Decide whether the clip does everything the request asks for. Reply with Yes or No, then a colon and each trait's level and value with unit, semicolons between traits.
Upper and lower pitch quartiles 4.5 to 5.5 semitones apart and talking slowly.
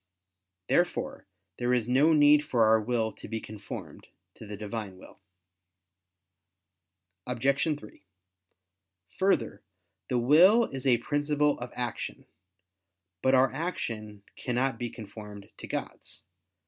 Yes: average, 4.8 semitones; slow, 120 wpm